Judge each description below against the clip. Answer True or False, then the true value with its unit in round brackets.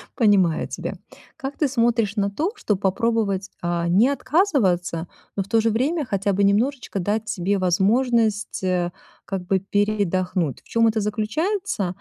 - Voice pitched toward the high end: True (205 Hz)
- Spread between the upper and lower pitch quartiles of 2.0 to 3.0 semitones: False (3.7 semitones)